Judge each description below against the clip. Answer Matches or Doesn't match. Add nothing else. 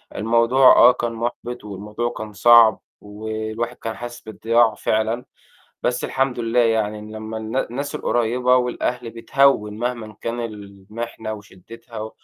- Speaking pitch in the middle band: Doesn't match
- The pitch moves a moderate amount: Doesn't match